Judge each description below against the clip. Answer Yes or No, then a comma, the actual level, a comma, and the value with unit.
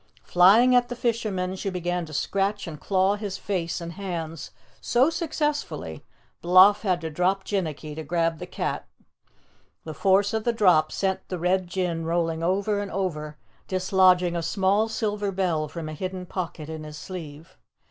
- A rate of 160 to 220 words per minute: Yes, average, 170 wpm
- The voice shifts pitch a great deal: No, average, 3.3 semitones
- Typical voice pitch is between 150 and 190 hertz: Yes, medium, 185 Hz